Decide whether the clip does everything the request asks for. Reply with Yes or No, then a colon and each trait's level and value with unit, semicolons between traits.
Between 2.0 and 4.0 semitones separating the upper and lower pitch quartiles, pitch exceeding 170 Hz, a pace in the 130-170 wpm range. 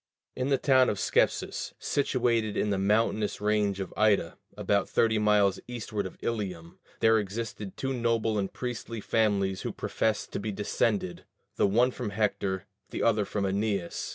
No: narrow, 2.5 semitones; low, 105 Hz; average, 160 wpm